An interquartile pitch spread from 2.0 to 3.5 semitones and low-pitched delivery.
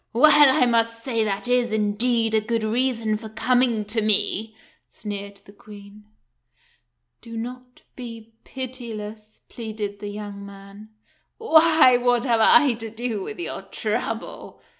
No: average, 2.7 semitones; high, 225 Hz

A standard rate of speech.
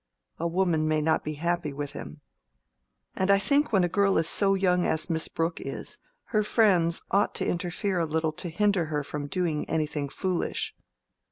Yes: average, 185 wpm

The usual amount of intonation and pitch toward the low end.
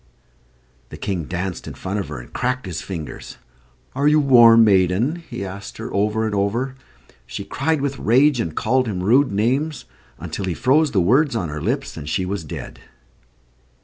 No: wide, 5.9 semitones; low, 110 Hz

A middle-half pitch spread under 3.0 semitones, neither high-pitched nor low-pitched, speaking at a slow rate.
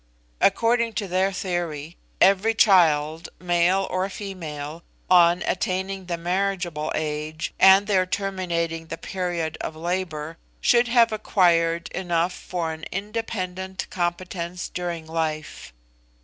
Yes: narrow, 2.6 semitones; medium, 180 Hz; slow, 115 wpm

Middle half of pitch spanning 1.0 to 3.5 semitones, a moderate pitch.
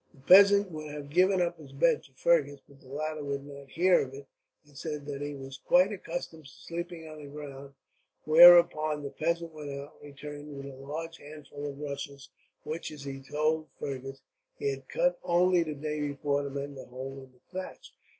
Yes: average, 3.0 semitones; medium, 150 Hz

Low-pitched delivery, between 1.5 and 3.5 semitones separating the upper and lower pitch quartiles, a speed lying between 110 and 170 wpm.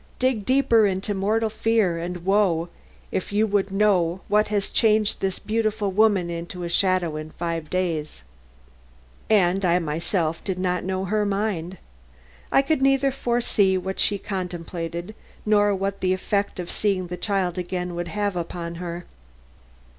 No: high, 190 Hz; average, 3.1 semitones; average, 155 wpm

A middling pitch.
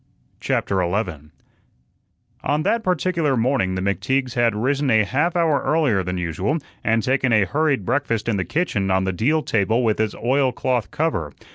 No: low, 120 Hz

